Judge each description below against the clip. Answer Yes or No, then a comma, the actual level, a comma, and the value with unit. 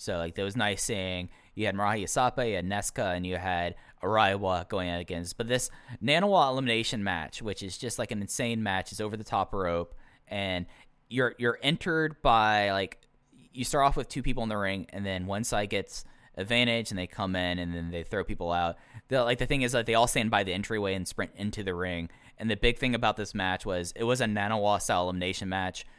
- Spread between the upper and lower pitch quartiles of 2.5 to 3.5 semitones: No, average, 4.5 semitones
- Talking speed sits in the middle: No, fast, 230 wpm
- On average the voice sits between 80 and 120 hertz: Yes, low, 105 Hz